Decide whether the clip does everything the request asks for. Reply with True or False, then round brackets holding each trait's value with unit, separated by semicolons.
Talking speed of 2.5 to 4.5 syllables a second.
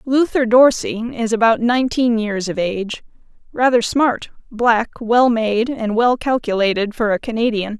True (4.4 syllables/s)